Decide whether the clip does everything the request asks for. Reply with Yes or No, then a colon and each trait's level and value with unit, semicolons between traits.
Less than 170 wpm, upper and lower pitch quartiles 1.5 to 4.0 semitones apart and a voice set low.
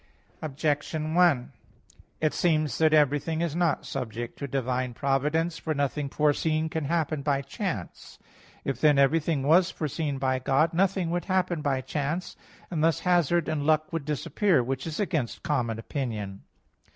No: average, 150 wpm; average, 3.2 semitones; medium, 150 Hz